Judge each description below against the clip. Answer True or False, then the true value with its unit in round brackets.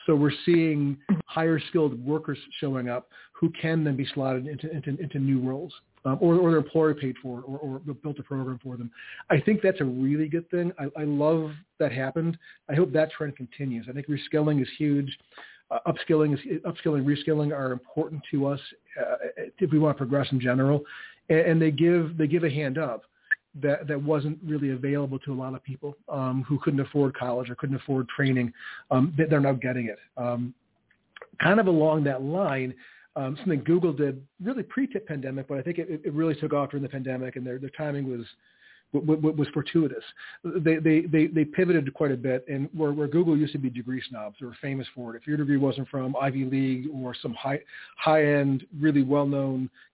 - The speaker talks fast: True (210 wpm)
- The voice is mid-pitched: True (145 Hz)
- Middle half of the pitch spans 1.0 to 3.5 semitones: True (2.9 semitones)